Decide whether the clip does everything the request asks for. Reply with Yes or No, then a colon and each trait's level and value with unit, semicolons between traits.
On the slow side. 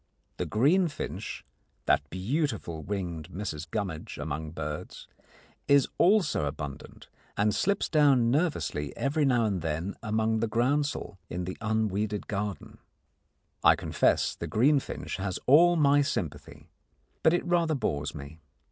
Yes: slow, 130 wpm